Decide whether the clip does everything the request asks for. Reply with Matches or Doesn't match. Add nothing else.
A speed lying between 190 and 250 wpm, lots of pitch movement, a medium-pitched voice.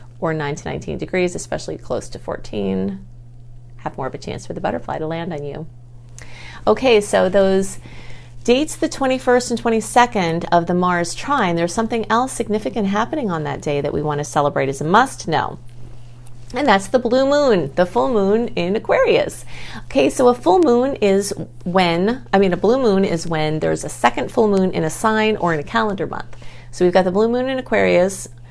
Matches